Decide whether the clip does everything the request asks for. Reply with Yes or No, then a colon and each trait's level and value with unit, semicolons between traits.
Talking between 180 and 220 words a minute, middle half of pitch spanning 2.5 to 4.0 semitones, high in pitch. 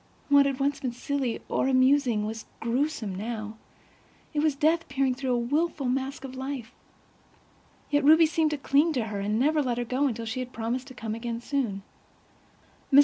Yes: average, 190 wpm; average, 3.4 semitones; very high, 260 Hz